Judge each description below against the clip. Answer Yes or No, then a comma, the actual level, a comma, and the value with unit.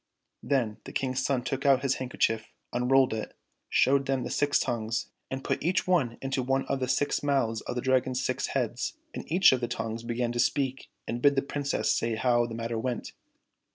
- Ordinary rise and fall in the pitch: No, narrow, 2.3 semitones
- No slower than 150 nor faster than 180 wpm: No, fast, 205 wpm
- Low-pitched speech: Yes, low, 130 Hz